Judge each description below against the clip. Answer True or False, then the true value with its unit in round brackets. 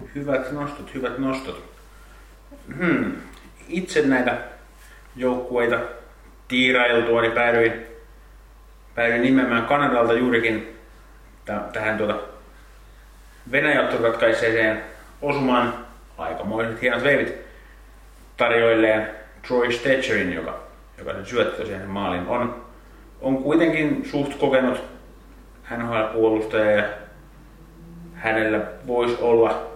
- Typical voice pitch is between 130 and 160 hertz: False (120 Hz)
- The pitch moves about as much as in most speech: True (3.2 semitones)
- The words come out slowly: True (90 wpm)